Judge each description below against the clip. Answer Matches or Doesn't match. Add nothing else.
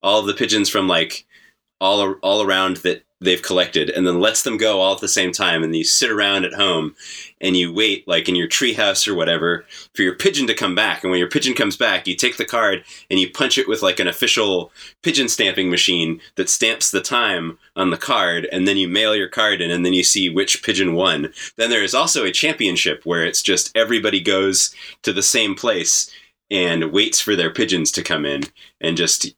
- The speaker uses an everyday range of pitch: Doesn't match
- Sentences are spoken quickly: Matches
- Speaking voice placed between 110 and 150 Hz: Doesn't match